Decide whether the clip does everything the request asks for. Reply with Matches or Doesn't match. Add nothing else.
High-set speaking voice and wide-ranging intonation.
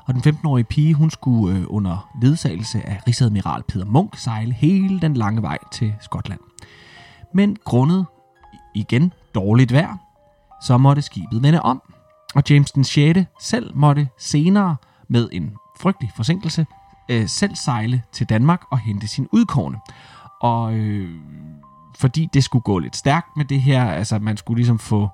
Doesn't match